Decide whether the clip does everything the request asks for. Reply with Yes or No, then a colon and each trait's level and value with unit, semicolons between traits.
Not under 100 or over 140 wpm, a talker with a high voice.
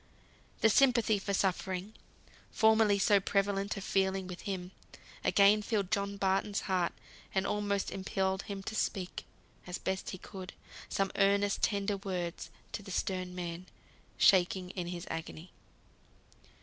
Yes: slow, 135 wpm; high, 195 Hz